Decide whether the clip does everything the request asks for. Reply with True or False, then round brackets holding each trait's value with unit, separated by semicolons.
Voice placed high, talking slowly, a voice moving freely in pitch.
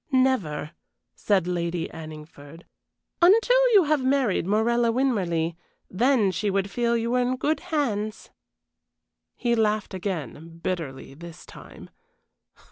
True (210 Hz; 120 wpm; 7.1 semitones)